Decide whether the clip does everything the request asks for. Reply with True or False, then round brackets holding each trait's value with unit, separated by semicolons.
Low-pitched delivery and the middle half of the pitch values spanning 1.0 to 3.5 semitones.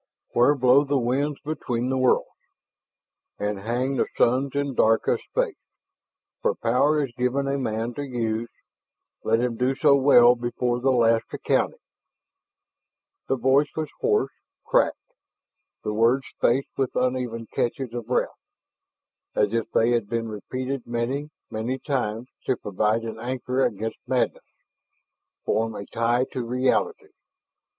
True (125 Hz; 2.9 semitones)